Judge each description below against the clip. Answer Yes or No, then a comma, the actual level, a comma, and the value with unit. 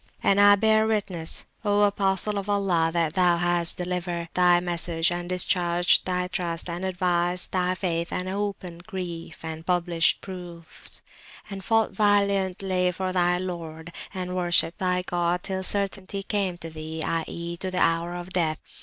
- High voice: No, medium, 180 Hz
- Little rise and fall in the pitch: Yes, narrow, 1.9 semitones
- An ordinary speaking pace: Yes, average, 155 wpm